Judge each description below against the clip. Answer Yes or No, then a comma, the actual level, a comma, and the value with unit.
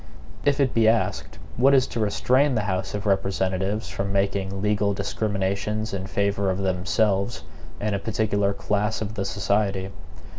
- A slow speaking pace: No, average, 155 wpm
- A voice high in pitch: No, low, 100 Hz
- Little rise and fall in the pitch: Yes, narrow, 1.9 semitones